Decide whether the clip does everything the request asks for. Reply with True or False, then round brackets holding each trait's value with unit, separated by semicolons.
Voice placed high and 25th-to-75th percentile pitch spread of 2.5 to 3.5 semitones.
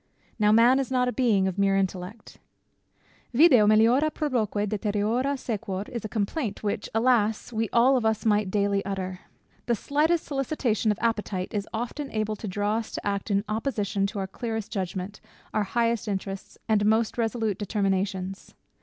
True (215 Hz; 2.9 semitones)